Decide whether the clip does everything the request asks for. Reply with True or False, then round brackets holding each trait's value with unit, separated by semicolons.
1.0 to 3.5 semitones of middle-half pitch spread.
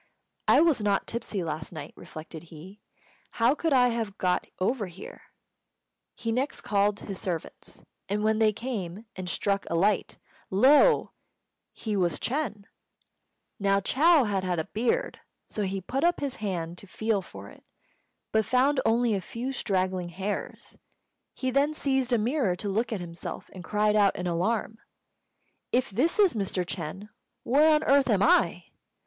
False (5.2 semitones)